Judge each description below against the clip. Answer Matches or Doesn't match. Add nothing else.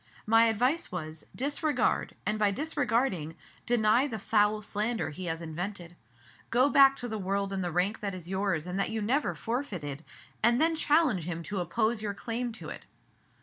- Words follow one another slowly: Doesn't match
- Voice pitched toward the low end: Doesn't match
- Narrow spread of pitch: Doesn't match